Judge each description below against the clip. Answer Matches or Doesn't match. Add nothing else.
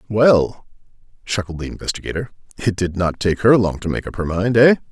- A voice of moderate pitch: Doesn't match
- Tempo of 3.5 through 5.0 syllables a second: Doesn't match